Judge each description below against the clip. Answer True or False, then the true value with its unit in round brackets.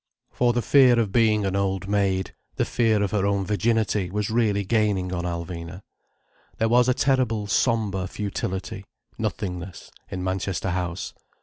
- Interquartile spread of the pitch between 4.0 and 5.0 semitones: False (3.1 semitones)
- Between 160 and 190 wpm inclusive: False (150 wpm)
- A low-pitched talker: True (100 Hz)